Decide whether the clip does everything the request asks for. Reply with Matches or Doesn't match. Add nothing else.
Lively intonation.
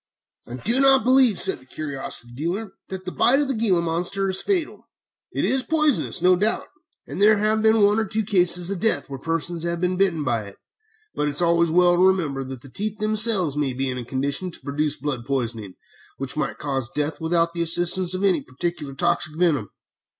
Matches